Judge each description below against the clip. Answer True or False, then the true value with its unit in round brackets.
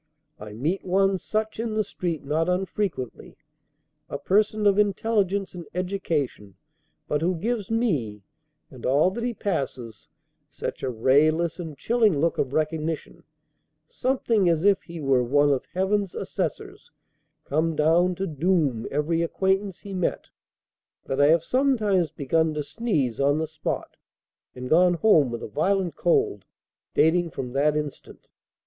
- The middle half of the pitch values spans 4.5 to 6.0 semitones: True (5.3 semitones)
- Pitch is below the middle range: False (170 Hz)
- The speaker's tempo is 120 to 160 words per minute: True (145 wpm)